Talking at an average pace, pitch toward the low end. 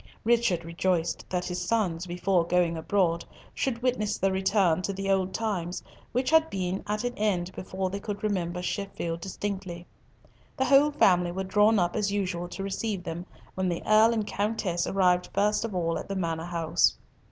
No: average, 180 wpm; high, 190 Hz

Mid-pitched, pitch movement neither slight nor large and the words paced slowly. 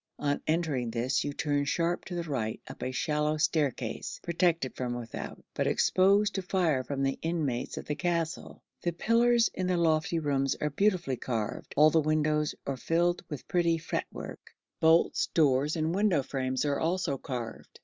No: medium, 155 Hz; average, 3.9 semitones; average, 170 wpm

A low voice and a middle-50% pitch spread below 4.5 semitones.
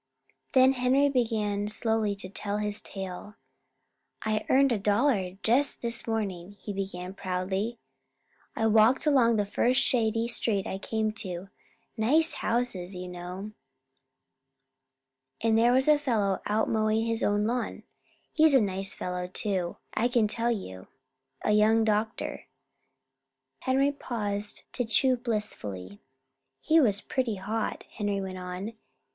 No: high, 215 Hz; average, 3.3 semitones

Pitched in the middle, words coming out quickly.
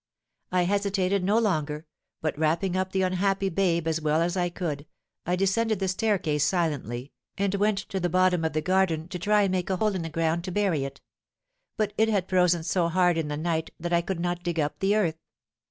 Yes: medium, 180 Hz; fast, 220 wpm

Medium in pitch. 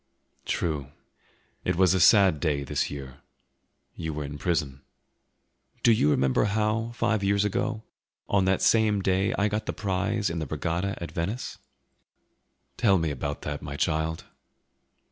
No: very low, 90 Hz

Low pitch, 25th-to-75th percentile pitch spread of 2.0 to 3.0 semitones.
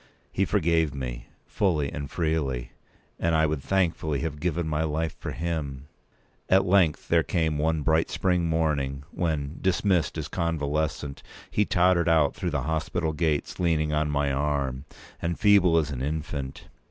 Yes: very low, 80 Hz; narrow, 2.6 semitones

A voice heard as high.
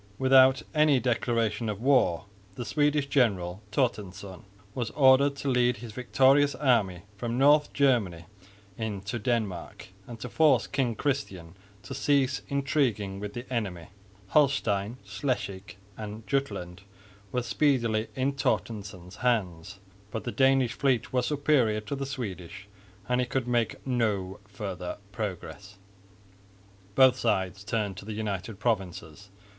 No: low, 115 Hz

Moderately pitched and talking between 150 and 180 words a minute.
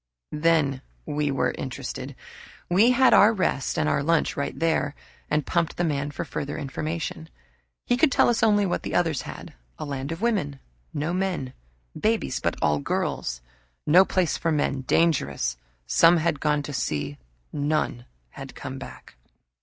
Yes: medium, 150 Hz; average, 160 wpm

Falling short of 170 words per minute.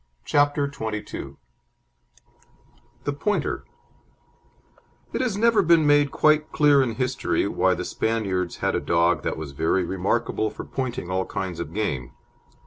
Yes: slow, 135 wpm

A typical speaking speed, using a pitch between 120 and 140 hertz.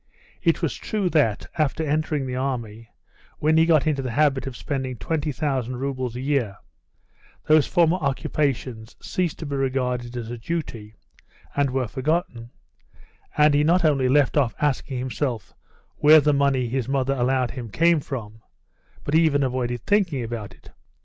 Yes: average, 160 wpm; low, 135 Hz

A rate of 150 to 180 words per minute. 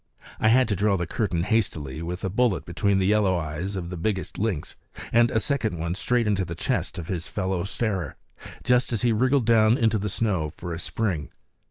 No: fast, 205 wpm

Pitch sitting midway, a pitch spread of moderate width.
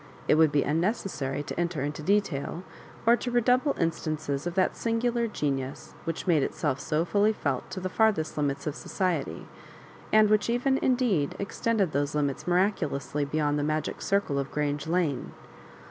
No: medium, 165 Hz; wide, 6.1 semitones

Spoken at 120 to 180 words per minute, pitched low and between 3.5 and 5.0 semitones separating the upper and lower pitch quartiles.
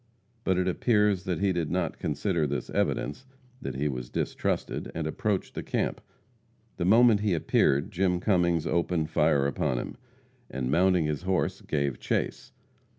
Yes: average, 155 wpm; very low, 85 Hz; average, 4.2 semitones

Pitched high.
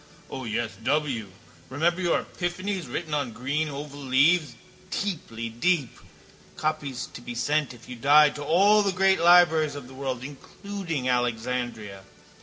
No: medium, 145 Hz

